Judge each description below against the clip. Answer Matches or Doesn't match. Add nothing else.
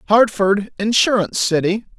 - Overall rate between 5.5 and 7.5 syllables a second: Doesn't match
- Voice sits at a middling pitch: Doesn't match